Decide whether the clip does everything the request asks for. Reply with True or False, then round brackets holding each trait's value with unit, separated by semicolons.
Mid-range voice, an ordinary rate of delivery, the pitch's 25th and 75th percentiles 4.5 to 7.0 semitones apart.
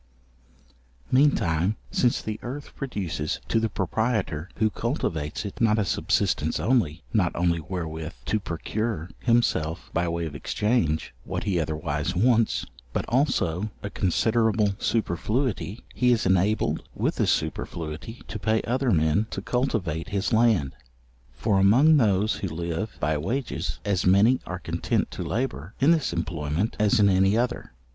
False (100 Hz; 150 wpm; 5.4 semitones)